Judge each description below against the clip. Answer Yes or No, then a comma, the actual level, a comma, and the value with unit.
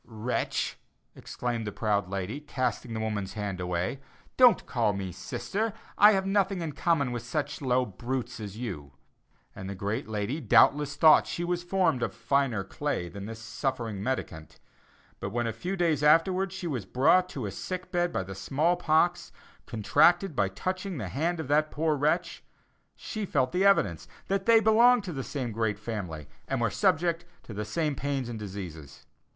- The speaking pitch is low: Yes, low, 130 Hz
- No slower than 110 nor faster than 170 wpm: No, average, 180 wpm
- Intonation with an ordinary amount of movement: No, wide, 8.6 semitones